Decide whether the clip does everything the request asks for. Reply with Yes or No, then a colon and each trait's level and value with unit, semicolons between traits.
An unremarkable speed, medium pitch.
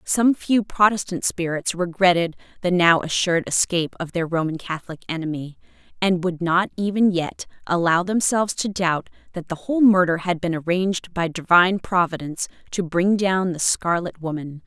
Yes: average, 160 wpm; medium, 175 Hz